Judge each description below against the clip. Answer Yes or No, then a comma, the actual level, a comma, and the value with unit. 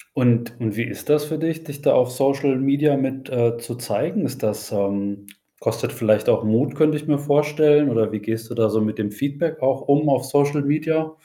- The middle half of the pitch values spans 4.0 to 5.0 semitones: Yes, average, 4.7 semitones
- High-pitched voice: No, low, 135 Hz